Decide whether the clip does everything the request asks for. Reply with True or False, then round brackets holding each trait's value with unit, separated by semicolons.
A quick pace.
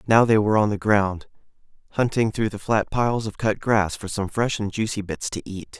True (230 wpm)